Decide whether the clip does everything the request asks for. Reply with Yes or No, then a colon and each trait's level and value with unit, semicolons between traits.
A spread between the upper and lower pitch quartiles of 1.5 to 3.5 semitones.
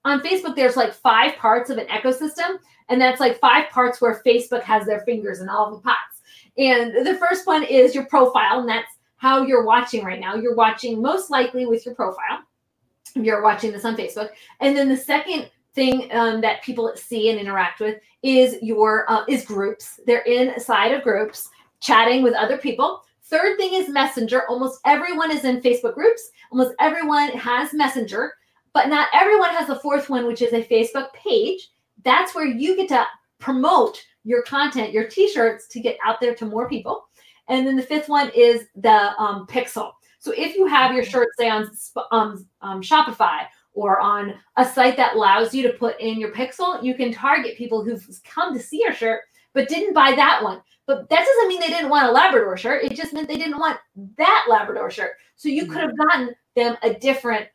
No: average, 4.2 semitones